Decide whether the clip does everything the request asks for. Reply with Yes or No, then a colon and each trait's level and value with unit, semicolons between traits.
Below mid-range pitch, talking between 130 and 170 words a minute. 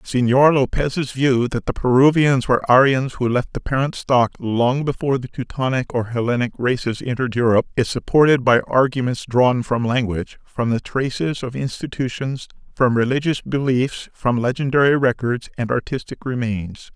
Yes: low, 125 Hz; average, 150 wpm